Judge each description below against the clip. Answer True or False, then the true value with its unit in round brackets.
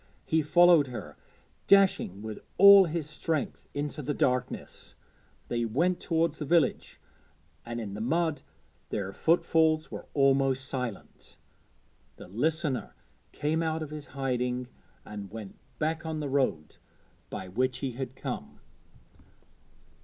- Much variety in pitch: False (4.5 semitones)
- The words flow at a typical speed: False (130 wpm)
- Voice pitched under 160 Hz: True (140 Hz)